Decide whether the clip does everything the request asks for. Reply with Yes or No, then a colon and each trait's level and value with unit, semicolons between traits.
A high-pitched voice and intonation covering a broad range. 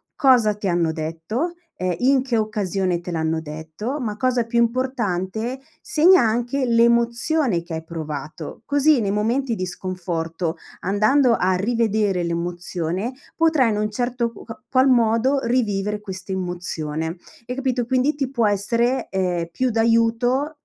Yes: high, 220 Hz; wide, 5.8 semitones